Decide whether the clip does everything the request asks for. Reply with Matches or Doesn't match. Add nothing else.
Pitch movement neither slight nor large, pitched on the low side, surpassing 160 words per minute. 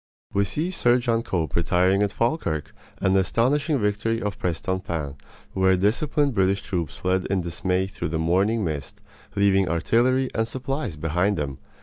Doesn't match